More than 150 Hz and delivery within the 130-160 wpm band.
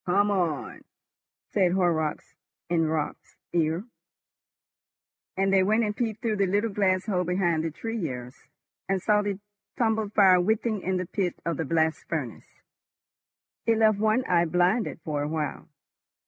Yes: medium, 185 Hz; average, 150 wpm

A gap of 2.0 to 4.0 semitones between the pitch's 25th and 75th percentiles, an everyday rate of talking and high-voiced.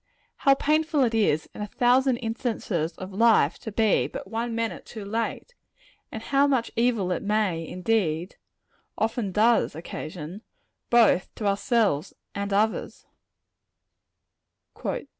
No: average, 3.7 semitones; slow, 125 wpm; high, 220 Hz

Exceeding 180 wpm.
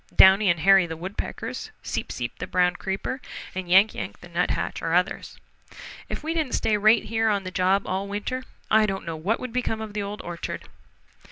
Yes: average, 200 wpm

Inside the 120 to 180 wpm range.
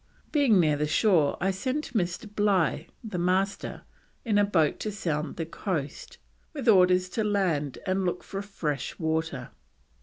Yes: average, 155 wpm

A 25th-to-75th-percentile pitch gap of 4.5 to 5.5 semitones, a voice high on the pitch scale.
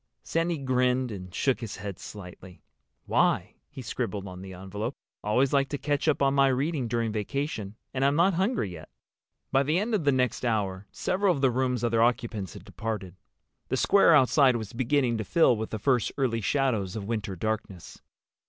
No: average, 4.8 semitones; low, 120 Hz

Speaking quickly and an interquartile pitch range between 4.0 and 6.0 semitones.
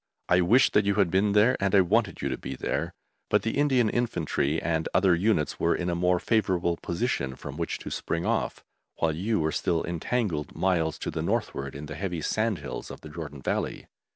Yes: fast, 210 wpm; average, 4.6 semitones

